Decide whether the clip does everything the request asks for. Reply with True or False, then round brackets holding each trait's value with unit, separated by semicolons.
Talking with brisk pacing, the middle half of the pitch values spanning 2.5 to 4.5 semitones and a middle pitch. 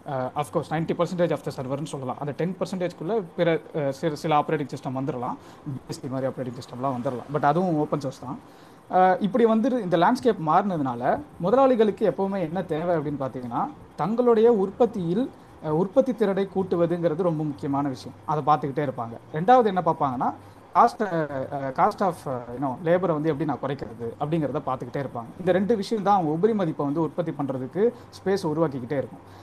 False (155 wpm; 5.1 semitones; 155 Hz)